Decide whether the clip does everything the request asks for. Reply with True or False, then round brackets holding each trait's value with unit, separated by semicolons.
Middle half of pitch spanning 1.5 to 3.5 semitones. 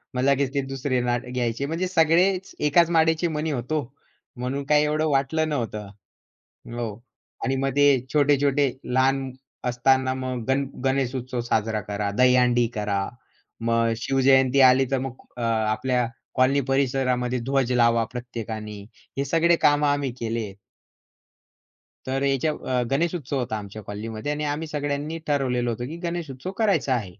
True (3.1 semitones)